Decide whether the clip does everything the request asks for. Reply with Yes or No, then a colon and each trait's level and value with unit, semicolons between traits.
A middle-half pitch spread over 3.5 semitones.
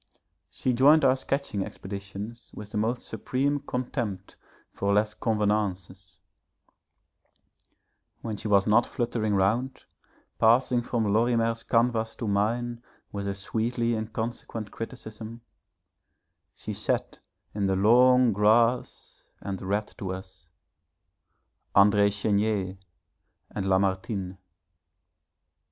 No: average, 3.0 semitones